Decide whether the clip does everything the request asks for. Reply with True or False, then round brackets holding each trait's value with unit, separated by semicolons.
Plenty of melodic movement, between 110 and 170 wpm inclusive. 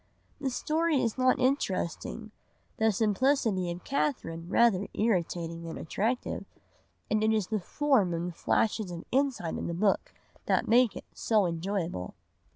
True (6.4 semitones; 150 wpm)